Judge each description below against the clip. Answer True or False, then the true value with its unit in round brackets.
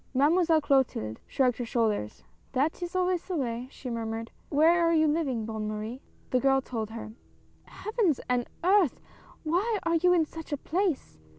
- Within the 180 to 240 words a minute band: True (190 wpm)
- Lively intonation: True (6.4 semitones)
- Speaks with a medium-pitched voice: False (280 Hz)